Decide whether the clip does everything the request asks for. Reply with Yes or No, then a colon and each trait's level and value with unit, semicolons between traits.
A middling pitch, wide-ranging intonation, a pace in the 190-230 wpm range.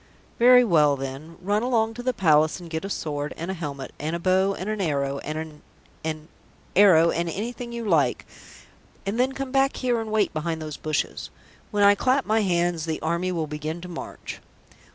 Yes: medium, 175 Hz; wide, 5.7 semitones; average, 200 wpm